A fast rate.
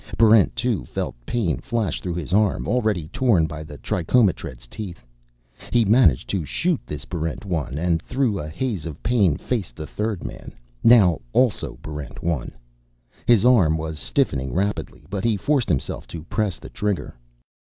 No: average, 165 wpm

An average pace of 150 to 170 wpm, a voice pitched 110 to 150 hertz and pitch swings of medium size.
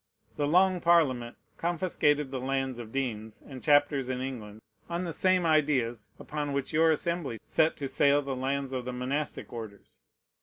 Yes: average, 165 wpm; medium, 140 Hz; average, 3.5 semitones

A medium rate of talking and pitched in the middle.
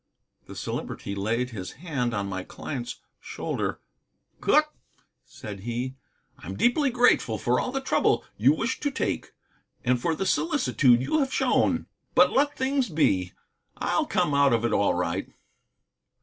No: average, 150 wpm; low, 130 Hz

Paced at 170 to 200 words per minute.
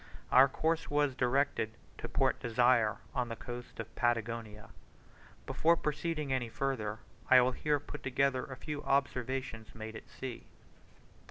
No: average, 145 wpm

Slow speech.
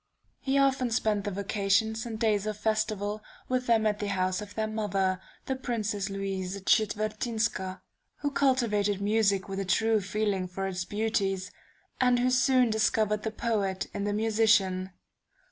No: average, 155 wpm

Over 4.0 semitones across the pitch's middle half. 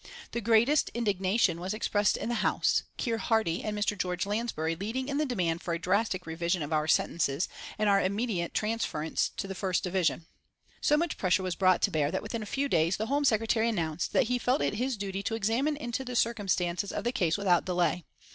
Yes: average, 4.7 semitones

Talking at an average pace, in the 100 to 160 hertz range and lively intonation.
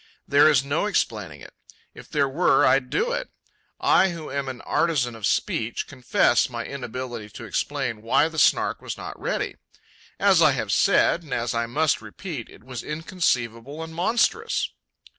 Yes: average, 170 wpm; medium, 140 Hz; wide, 5.7 semitones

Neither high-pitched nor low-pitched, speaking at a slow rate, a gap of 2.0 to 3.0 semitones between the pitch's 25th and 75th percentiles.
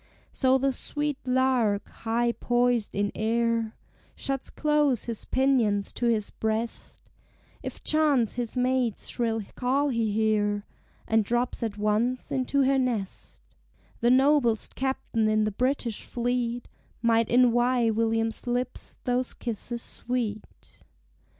No: high, 240 Hz; slow, 125 wpm; narrow, 2.5 semitones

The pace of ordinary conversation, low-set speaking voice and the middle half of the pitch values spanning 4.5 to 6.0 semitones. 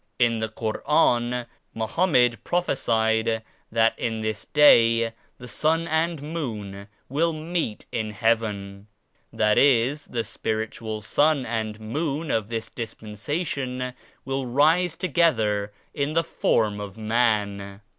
No: slow, 125 wpm; low, 115 Hz; average, 5.1 semitones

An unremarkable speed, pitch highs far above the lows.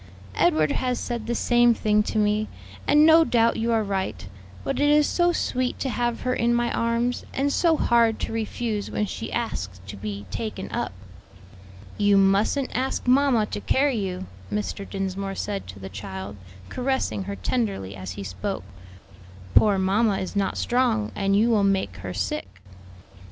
No: average, 170 wpm; average, 4.2 semitones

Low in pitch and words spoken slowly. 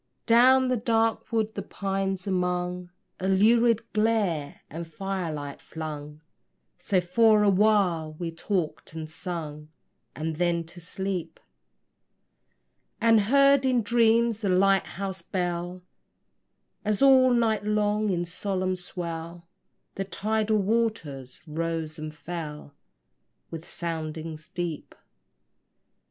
No: medium, 185 Hz; slow, 115 wpm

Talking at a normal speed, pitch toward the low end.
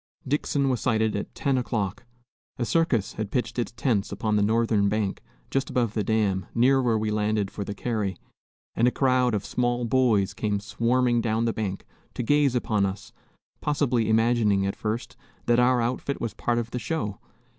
Yes: average, 190 wpm; low, 115 Hz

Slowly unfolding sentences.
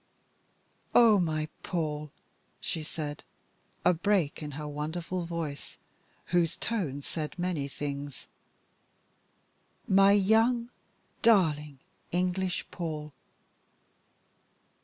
Yes: slow, 85 wpm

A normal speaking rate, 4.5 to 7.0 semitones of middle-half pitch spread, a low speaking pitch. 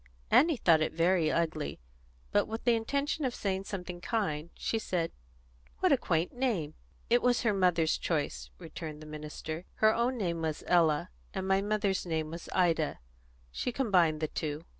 No: average, 170 wpm; wide, 5.5 semitones; medium, 175 Hz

